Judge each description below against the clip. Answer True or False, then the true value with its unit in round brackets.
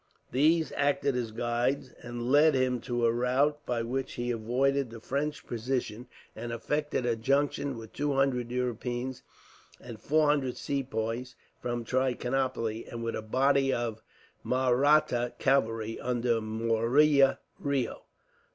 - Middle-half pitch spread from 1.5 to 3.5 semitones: True (2.8 semitones)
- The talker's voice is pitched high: False (125 Hz)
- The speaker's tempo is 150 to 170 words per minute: False (135 wpm)